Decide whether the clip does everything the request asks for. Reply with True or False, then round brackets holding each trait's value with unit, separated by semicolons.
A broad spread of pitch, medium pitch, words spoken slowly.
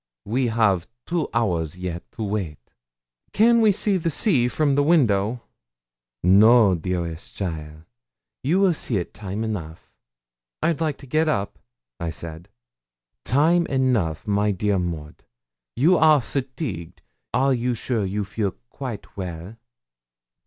False (7.3 semitones; 110 Hz; 130 wpm)